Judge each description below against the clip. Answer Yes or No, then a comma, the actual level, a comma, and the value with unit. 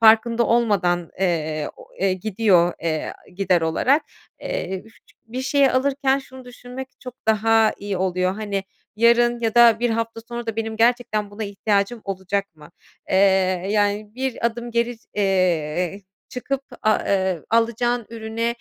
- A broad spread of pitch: No, average, 3.8 semitones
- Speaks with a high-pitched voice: Yes, high, 220 Hz